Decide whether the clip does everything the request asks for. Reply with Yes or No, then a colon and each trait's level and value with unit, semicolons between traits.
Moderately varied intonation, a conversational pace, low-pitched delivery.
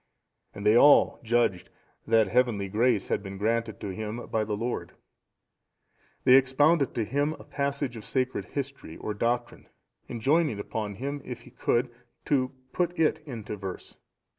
Yes: average, 4.3 semitones; average, 155 wpm; low, 120 Hz